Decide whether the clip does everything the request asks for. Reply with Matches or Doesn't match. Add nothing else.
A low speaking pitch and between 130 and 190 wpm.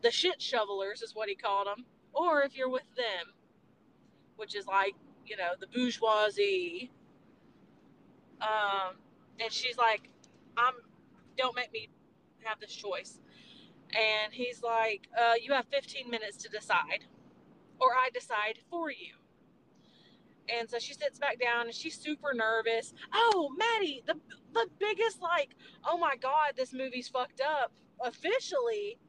Doesn't match